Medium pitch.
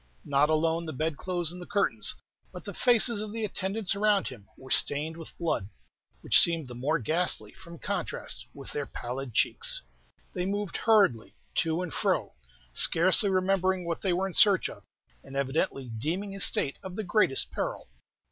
Yes: medium, 170 Hz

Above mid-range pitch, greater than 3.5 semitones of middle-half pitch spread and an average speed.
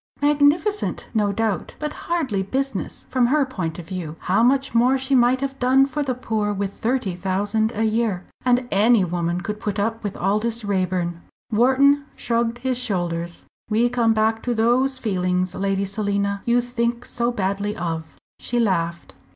Yes: high, 225 Hz; average, 4.4 semitones; average, 165 wpm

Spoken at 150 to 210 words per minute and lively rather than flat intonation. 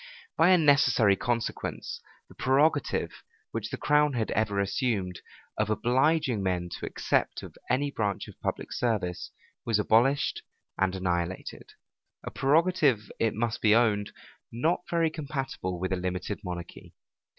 No: average, 140 wpm; wide, 6.6 semitones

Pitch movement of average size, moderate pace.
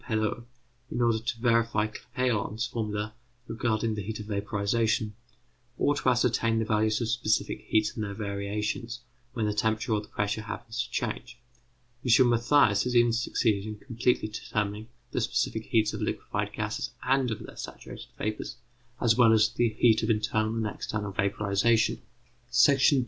No: narrow, 1.9 semitones; average, 165 wpm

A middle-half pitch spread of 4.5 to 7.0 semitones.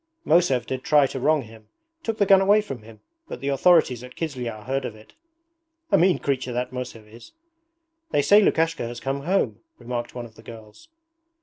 Yes: wide, 5.6 semitones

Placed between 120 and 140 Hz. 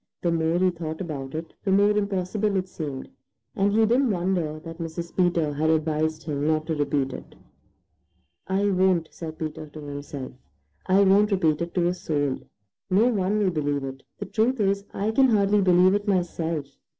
No: medium, 175 Hz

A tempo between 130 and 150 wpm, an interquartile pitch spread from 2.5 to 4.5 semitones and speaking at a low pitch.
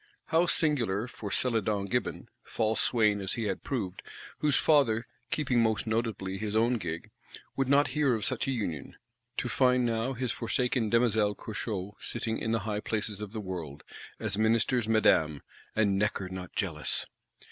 No: average, 160 wpm; average, 3.3 semitones; low, 110 Hz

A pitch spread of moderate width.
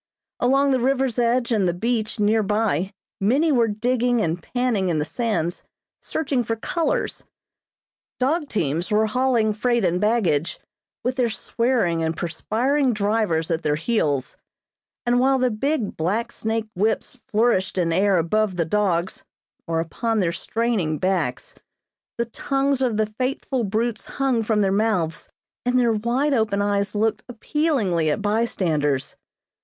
Yes: average, 4.9 semitones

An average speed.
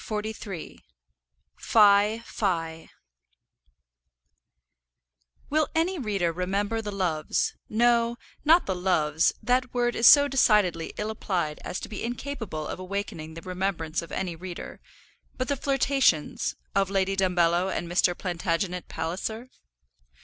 No: slow, 120 wpm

